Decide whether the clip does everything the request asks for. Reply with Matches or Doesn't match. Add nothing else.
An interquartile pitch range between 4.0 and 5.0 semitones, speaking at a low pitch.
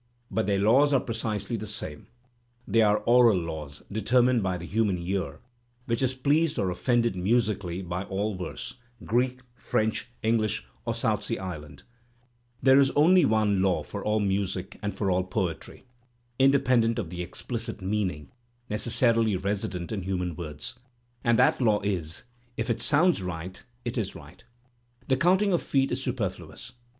Matches